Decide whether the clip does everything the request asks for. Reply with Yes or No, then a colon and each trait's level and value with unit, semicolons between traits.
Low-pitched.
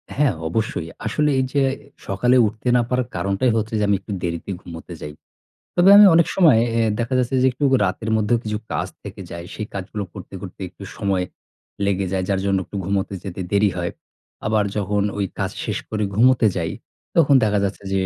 Yes: low, 105 Hz